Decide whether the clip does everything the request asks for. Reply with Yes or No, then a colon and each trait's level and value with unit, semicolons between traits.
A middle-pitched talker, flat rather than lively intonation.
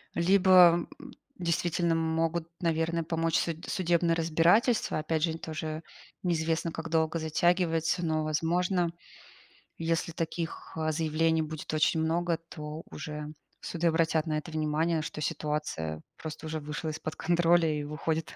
Yes: medium, 160 Hz; narrow, 1.4 semitones